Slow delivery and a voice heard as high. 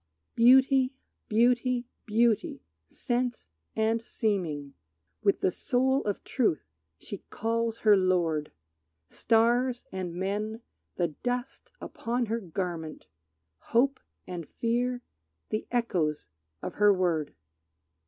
Yes: slow, 105 wpm; high, 225 Hz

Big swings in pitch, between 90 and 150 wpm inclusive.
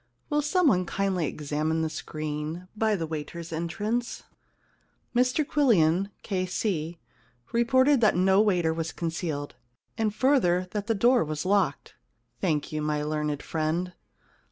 Yes: wide, 5.7 semitones; slow, 135 wpm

